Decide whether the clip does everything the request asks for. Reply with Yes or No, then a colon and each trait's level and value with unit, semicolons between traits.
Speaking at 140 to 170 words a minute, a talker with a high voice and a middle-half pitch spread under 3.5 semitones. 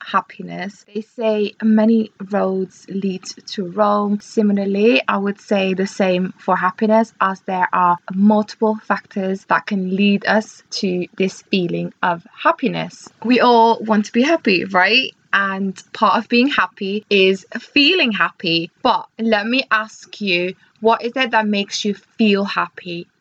Yes: average, 150 wpm; high, 205 Hz; narrow, 2.6 semitones